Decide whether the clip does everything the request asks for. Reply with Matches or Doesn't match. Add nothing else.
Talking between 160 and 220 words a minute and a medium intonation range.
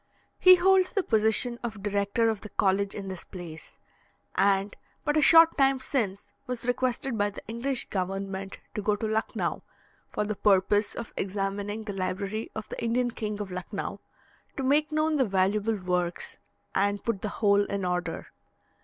Matches